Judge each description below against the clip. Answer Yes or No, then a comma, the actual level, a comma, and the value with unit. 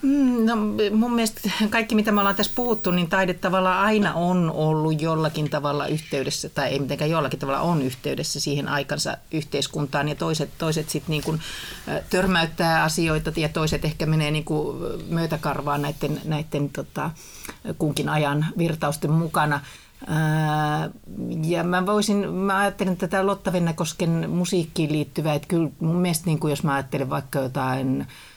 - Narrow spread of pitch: No, average, 3.7 semitones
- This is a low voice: No, medium, 160 Hz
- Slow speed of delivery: No, average, 145 wpm